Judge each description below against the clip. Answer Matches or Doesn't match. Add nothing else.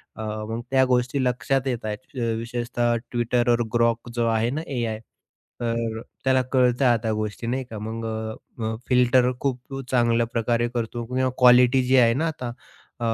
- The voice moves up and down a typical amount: Doesn't match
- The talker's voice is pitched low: Matches